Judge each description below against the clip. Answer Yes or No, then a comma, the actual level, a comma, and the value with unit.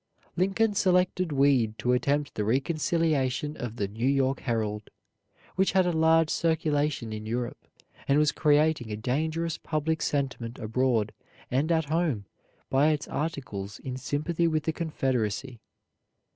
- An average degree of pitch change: Yes, average, 4.8 semitones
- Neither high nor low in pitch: Yes, medium, 145 Hz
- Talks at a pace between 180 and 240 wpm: No, average, 140 wpm